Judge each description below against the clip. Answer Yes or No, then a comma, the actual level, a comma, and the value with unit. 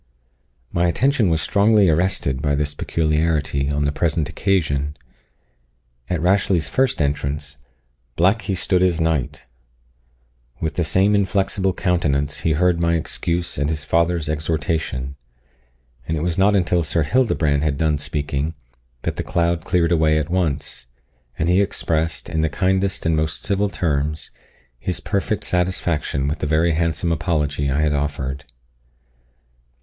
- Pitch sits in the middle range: No, very low, 80 Hz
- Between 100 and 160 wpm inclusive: Yes, average, 145 wpm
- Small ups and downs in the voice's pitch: No, average, 3.4 semitones